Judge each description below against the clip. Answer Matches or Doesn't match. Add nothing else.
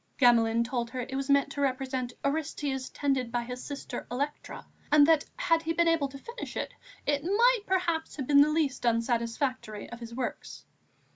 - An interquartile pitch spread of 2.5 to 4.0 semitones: Matches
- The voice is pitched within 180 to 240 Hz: Doesn't match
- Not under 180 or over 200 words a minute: Matches